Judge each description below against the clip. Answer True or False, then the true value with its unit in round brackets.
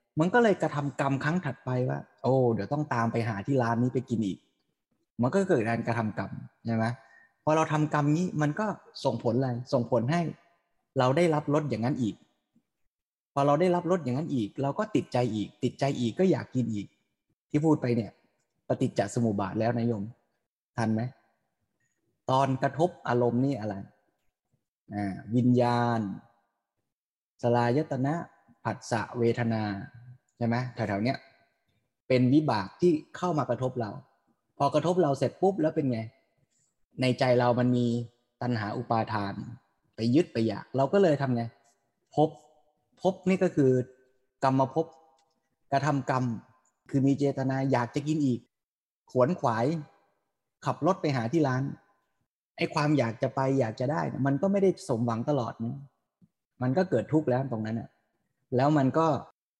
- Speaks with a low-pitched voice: True (130 Hz)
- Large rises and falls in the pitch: False (4.2 semitones)